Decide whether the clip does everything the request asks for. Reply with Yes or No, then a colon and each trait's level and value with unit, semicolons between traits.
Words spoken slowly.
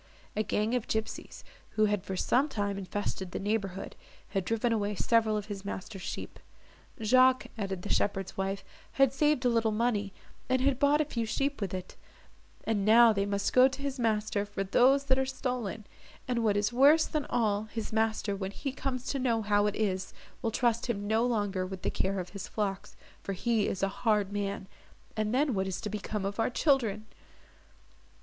No: average, 200 wpm